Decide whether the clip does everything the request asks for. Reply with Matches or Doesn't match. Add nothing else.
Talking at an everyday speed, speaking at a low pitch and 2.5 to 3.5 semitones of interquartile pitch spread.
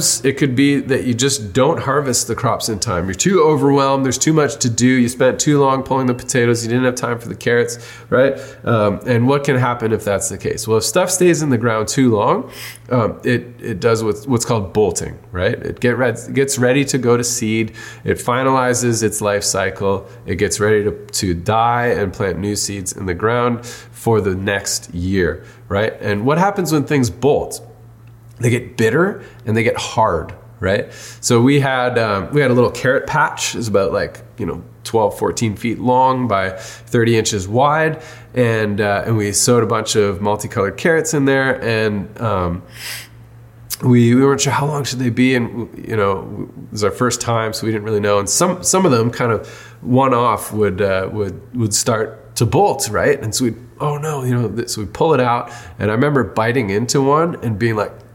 Doesn't match